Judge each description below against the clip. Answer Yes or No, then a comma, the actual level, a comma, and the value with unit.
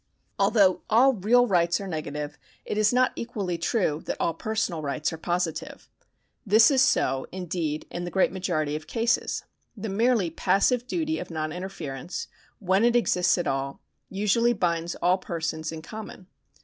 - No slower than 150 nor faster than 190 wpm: Yes, average, 160 wpm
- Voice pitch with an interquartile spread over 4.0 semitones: Yes, average, 5.2 semitones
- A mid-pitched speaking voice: Yes, medium, 180 Hz